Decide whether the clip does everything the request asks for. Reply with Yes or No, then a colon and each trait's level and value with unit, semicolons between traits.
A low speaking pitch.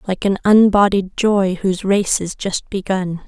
No: high, 195 Hz